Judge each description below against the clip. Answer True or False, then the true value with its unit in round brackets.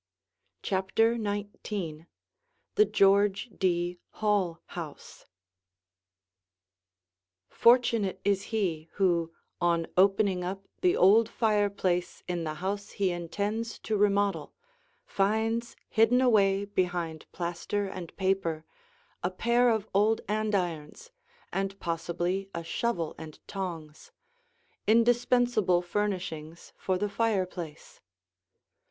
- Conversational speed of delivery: False (100 wpm)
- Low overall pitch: False (195 Hz)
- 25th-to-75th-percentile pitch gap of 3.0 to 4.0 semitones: True (3.5 semitones)